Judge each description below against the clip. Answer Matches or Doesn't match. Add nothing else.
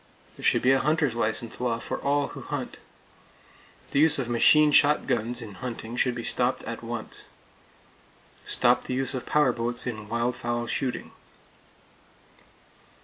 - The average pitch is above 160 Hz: Doesn't match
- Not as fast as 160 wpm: Matches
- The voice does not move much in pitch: Matches